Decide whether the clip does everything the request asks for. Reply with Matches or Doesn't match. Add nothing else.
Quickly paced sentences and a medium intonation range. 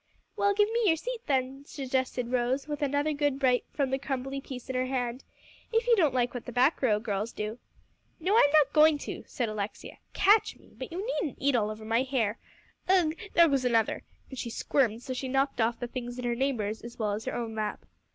Matches